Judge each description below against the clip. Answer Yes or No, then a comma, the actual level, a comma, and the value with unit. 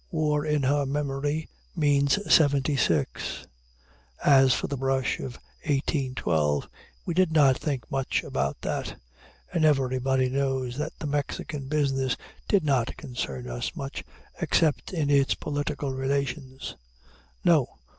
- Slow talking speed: Yes, slow, 125 wpm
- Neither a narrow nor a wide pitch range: No, narrow, 2.2 semitones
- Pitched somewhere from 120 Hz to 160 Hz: Yes, medium, 140 Hz